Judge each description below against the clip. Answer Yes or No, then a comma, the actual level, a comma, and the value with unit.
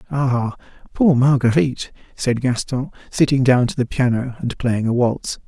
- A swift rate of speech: No, average, 155 wpm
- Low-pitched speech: Yes, low, 125 Hz